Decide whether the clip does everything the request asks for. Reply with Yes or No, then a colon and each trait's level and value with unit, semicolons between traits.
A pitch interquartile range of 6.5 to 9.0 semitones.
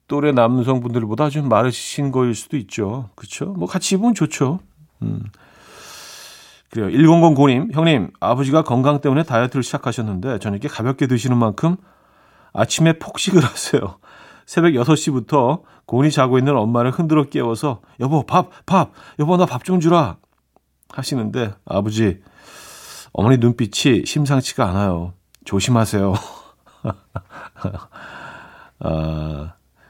No: wide, 5.4 semitones